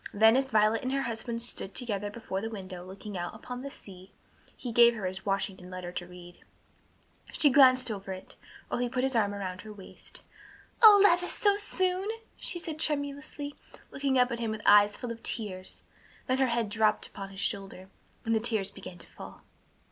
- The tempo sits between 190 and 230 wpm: Yes, average, 195 wpm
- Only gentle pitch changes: No, average, 4.9 semitones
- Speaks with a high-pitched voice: Yes, high, 220 Hz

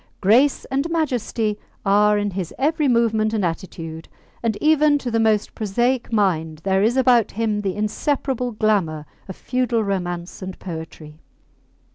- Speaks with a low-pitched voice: No, high, 215 Hz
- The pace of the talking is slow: No, average, 145 wpm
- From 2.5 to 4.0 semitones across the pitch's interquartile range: No, average, 4.5 semitones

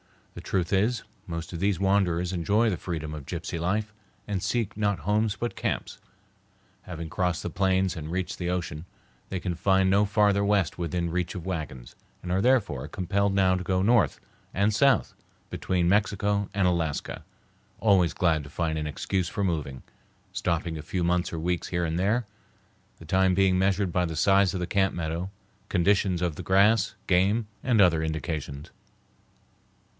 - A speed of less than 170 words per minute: No, average, 175 wpm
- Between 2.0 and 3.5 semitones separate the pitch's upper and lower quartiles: Yes, average, 3.1 semitones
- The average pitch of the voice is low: Yes, very low, 90 Hz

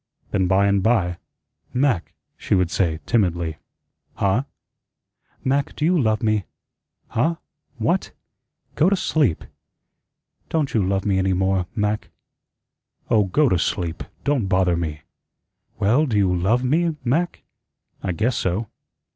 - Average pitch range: No, wide, 5.9 semitones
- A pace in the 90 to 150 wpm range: Yes, slow, 135 wpm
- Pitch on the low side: Yes, low, 105 Hz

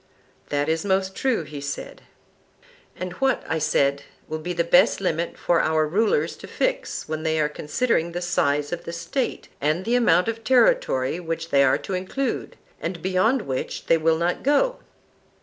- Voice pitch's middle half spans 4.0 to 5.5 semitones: Yes, average, 5.2 semitones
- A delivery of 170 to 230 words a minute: Yes, average, 180 wpm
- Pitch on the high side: No, medium, 170 Hz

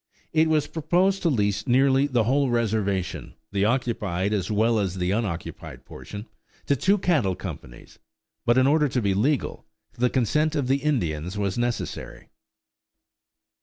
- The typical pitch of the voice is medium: No, low, 120 Hz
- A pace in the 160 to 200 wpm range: No, average, 150 wpm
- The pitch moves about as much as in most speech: No, wide, 5.9 semitones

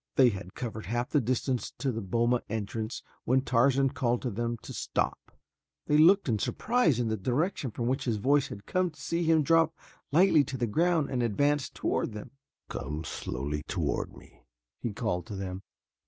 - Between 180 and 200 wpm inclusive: Yes, average, 185 wpm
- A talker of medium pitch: No, low, 125 Hz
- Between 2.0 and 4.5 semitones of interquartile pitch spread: No, average, 5.1 semitones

